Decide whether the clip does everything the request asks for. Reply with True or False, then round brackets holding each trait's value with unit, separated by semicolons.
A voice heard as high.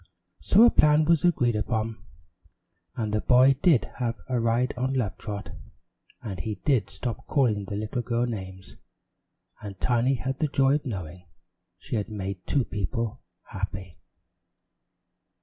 False (115 Hz)